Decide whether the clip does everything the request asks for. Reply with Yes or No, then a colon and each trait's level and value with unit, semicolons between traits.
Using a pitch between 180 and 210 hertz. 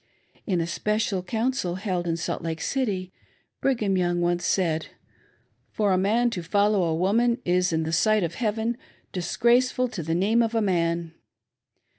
Yes: high, 190 Hz